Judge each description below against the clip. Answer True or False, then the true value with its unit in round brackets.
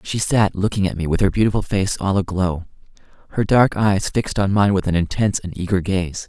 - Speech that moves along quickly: True (220 wpm)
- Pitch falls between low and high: False (95 Hz)